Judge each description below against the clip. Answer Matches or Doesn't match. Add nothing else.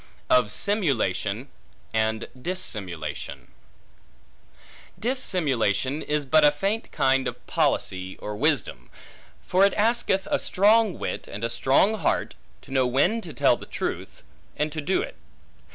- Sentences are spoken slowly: Matches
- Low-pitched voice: Doesn't match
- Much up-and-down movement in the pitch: Matches